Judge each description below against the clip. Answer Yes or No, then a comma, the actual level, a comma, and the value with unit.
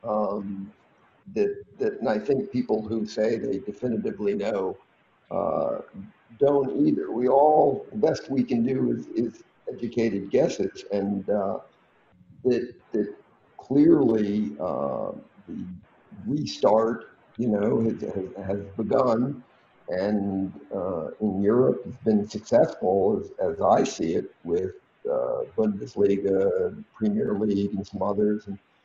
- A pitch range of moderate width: No, wide, 7.1 semitones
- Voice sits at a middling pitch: No, low, 110 Hz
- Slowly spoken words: Yes, slow, 125 wpm